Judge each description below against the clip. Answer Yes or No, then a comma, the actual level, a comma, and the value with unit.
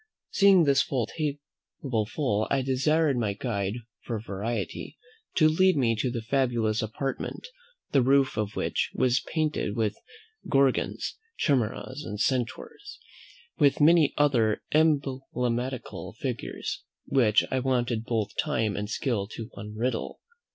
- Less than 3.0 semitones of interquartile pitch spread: No, average, 4.4 semitones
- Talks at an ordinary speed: No, slow, 125 wpm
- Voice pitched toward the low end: Yes, low, 130 Hz